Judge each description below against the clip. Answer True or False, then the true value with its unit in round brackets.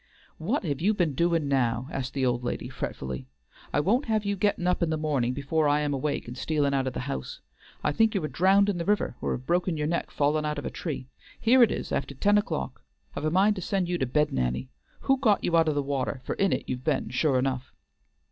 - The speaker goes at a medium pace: False (250 wpm)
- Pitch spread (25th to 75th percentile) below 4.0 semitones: False (5.5 semitones)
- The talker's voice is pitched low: False (150 Hz)